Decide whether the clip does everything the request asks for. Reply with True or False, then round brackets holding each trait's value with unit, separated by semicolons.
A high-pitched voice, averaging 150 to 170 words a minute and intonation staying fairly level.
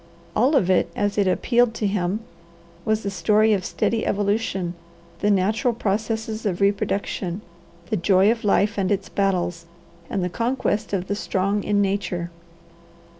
True (205 Hz; 155 wpm; 2.2 semitones)